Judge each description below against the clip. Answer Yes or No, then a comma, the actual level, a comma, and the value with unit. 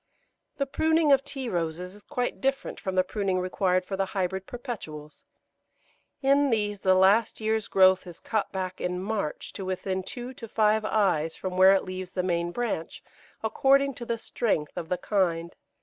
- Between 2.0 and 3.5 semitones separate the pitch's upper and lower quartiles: No, average, 4.0 semitones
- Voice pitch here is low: No, high, 195 Hz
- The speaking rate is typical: Yes, average, 180 wpm